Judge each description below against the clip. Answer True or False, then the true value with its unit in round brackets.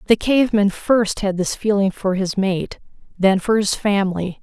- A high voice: True (200 Hz)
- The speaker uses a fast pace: False (175 wpm)